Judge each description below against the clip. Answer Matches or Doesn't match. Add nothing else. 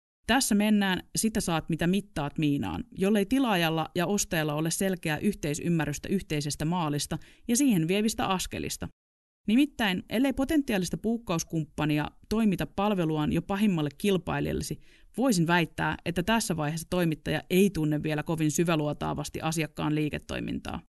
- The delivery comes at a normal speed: Matches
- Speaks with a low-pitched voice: Doesn't match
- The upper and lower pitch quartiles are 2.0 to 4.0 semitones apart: Doesn't match